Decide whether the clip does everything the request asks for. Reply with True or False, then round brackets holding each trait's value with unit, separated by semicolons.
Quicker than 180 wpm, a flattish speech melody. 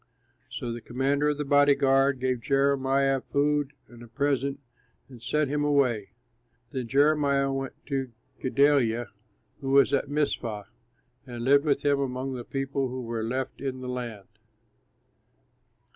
False (145 wpm; 2.0 semitones)